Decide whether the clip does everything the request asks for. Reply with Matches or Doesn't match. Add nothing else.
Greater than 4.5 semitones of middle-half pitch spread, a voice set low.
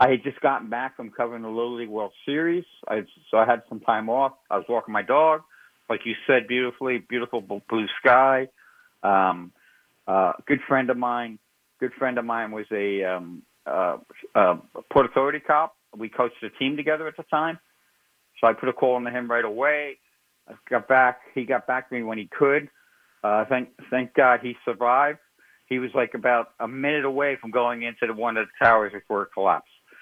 Doesn't match